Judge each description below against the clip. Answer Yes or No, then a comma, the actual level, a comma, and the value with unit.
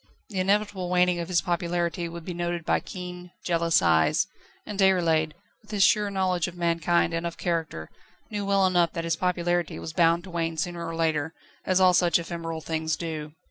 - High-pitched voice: No, medium, 170 Hz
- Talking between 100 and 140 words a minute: No, average, 190 wpm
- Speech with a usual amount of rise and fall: No, narrow, 1.7 semitones